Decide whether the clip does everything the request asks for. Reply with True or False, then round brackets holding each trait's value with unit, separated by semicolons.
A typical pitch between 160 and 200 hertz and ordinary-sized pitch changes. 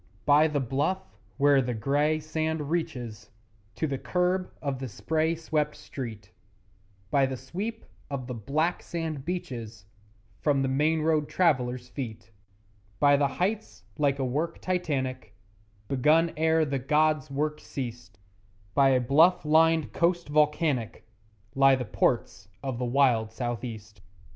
False (140 Hz; 4.0 semitones)